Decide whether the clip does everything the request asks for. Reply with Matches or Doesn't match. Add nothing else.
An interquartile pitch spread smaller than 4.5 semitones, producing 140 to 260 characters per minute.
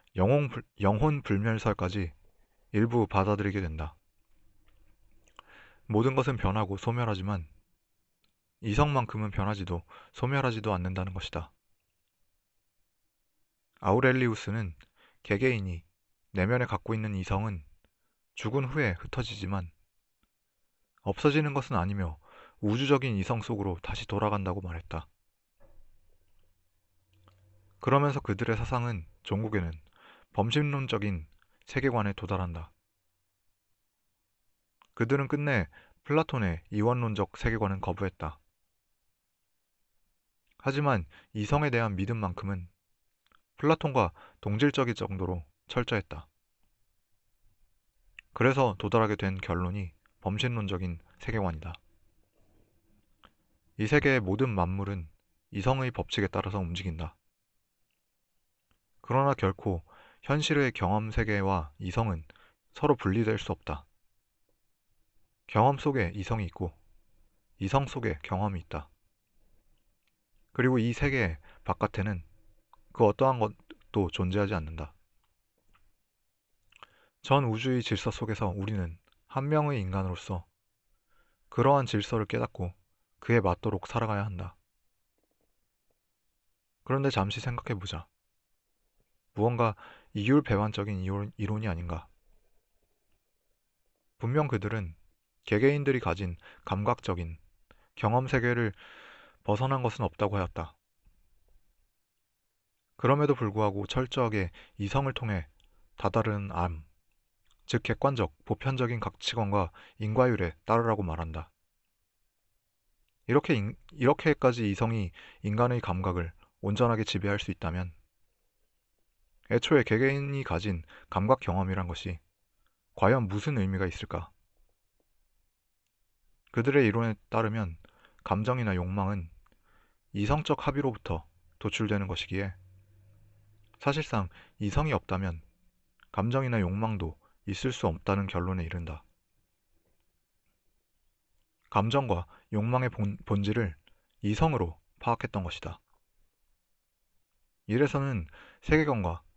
Matches